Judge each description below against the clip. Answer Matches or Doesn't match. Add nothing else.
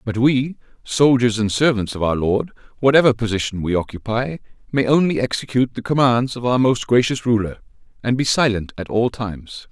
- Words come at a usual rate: Matches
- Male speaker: Matches